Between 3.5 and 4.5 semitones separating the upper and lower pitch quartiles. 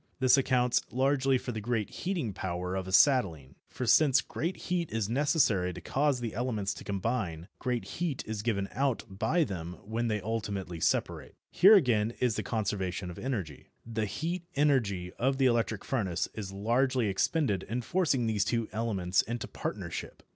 No: average, 5.1 semitones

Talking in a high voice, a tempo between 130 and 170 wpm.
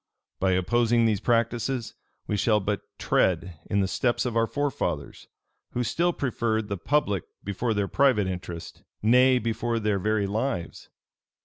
No: low, 110 Hz; average, 145 wpm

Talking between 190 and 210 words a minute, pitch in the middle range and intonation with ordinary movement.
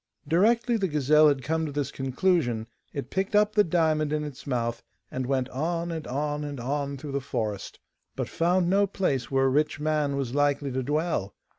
Yes: average, 195 wpm; medium, 145 Hz; average, 3.8 semitones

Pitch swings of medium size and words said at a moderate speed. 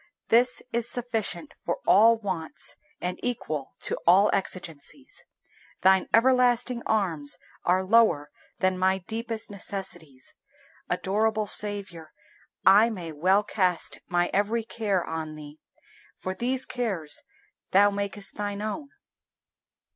No: average, 4.3 semitones; slow, 115 wpm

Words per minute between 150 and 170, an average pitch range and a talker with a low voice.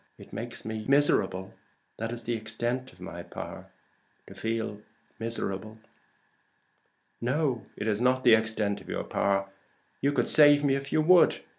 Yes: average, 155 wpm; average, 3.7 semitones; low, 115 Hz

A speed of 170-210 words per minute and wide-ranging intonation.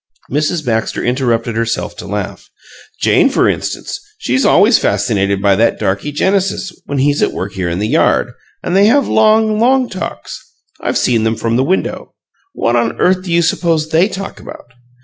Yes: average, 180 wpm; wide, 8.8 semitones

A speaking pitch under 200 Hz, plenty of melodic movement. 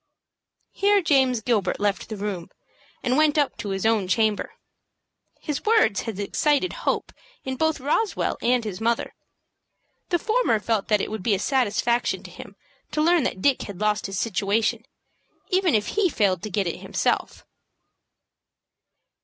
No: high, 230 Hz; wide, 6.3 semitones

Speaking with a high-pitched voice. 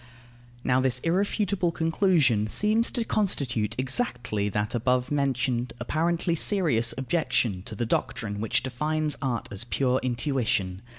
No: low, 130 Hz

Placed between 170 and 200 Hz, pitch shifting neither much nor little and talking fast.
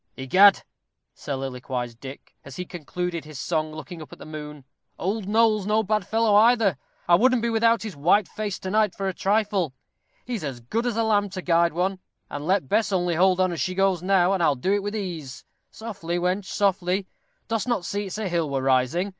Yes: medium, 185 Hz; average, 4.9 semitones; fast, 210 wpm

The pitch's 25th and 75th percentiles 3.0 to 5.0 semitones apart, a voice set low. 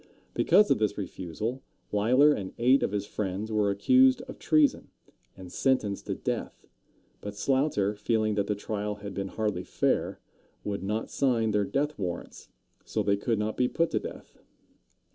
Yes: average, 4.4 semitones; low, 105 Hz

